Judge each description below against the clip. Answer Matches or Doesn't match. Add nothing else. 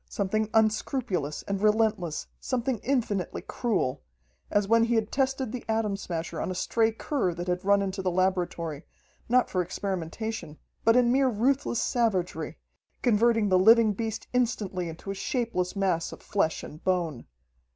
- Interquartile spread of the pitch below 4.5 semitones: Matches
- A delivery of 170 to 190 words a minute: Doesn't match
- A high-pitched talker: Matches